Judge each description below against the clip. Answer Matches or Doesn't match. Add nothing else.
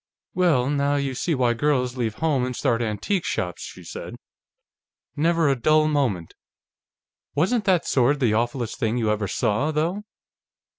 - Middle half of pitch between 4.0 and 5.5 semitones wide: Matches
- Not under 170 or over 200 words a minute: Doesn't match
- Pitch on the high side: Doesn't match